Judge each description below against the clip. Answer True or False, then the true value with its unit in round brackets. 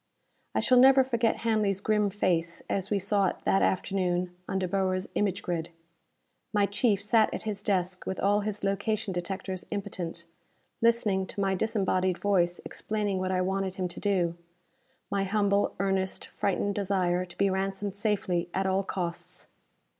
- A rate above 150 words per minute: True (160 wpm)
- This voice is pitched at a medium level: False (195 Hz)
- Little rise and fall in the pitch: True (1.9 semitones)